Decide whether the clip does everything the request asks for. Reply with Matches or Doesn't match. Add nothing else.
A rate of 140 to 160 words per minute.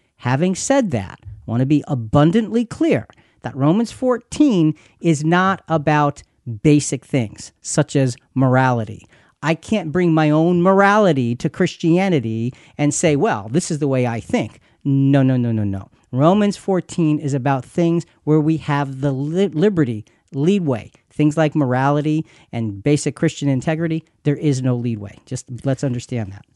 Matches